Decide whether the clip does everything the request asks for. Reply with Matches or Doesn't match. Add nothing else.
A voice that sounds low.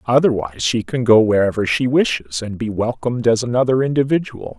Matches